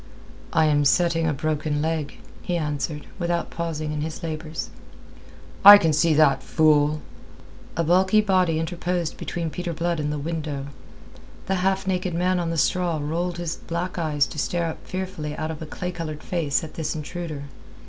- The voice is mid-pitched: Yes, medium, 165 Hz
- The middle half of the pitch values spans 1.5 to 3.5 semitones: Yes, narrow, 2.5 semitones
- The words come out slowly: No, average, 175 wpm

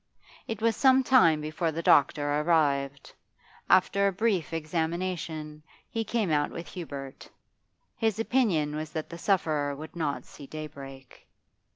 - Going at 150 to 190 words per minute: No, average, 140 wpm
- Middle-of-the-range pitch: Yes, medium, 160 Hz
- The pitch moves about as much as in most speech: Yes, average, 4.5 semitones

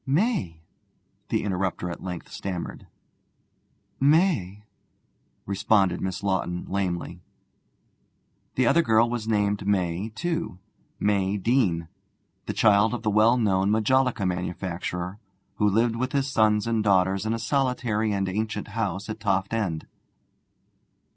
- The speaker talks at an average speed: No, slow, 120 wpm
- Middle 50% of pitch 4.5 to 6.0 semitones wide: No, average, 3.4 semitones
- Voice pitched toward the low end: Yes, low, 105 Hz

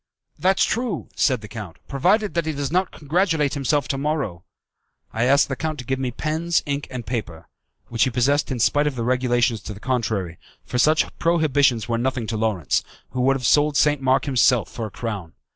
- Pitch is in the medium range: No, low, 130 Hz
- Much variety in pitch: No, average, 4.4 semitones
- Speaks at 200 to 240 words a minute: Yes, fast, 205 wpm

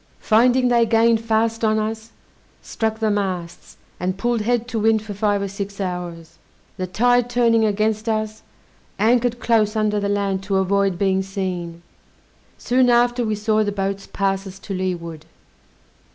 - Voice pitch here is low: No, high, 210 Hz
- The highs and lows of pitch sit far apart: No, average, 2.8 semitones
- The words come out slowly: No, average, 160 wpm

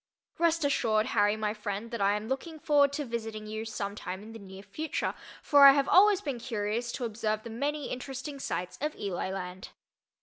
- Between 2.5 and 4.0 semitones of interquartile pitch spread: No, average, 5.2 semitones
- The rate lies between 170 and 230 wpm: Yes, average, 200 wpm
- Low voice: No, high, 225 Hz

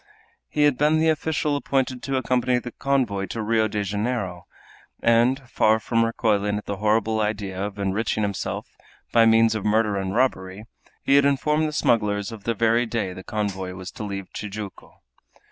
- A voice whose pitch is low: Yes, low, 110 Hz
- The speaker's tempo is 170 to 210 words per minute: Yes, average, 180 wpm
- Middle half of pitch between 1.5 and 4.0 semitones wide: Yes, average, 3.7 semitones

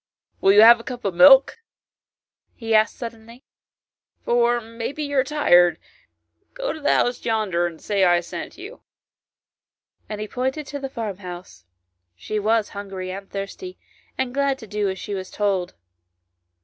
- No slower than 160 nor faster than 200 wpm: Yes, average, 175 wpm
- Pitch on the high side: Yes, high, 220 Hz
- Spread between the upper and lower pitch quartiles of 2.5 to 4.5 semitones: No, average, 5.1 semitones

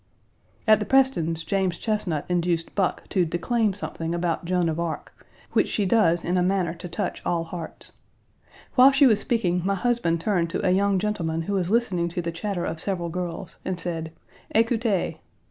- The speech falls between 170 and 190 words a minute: Yes, average, 180 wpm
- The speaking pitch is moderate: Yes, medium, 180 Hz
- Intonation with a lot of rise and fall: No, average, 3.7 semitones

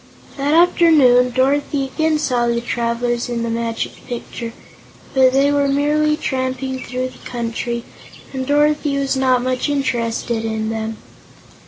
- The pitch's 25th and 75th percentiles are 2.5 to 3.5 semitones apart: Yes, average, 3.1 semitones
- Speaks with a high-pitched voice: Yes, very high, 255 Hz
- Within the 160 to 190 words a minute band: No, average, 140 wpm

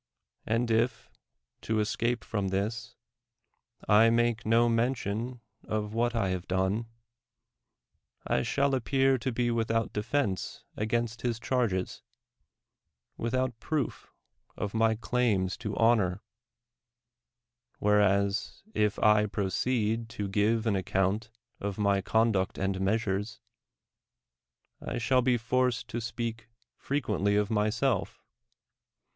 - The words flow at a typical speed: No, slow, 110 wpm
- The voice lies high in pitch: No, low, 110 Hz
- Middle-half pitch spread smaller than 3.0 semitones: Yes, narrow, 2.6 semitones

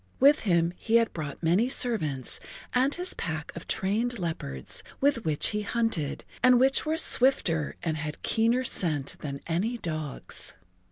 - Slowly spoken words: No, average, 155 wpm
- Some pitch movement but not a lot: No, wide, 7.6 semitones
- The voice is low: No, high, 190 Hz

